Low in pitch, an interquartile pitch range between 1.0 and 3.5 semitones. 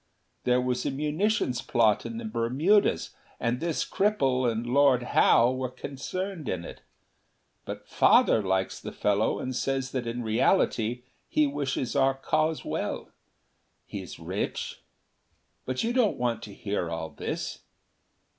No: low, 130 Hz; average, 4.4 semitones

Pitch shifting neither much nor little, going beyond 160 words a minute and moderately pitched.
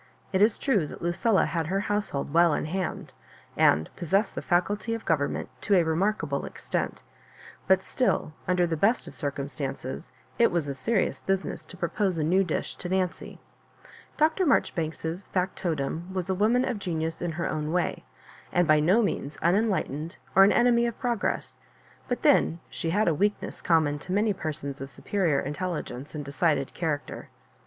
Yes: average, 4.5 semitones; average, 180 wpm; medium, 175 Hz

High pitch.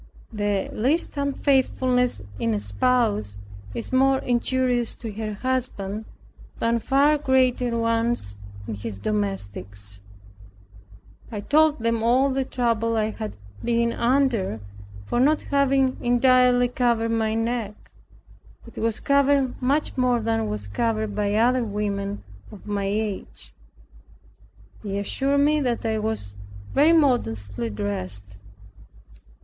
Yes: high, 230 Hz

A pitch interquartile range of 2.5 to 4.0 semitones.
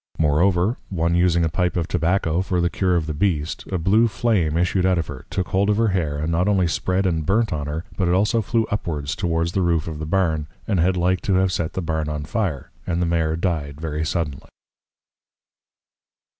Yes: average, 3.1 semitones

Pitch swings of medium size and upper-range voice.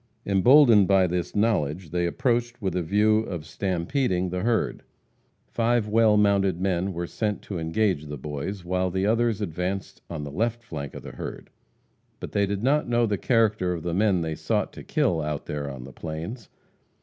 No: average, 4.4 semitones; very low, 95 Hz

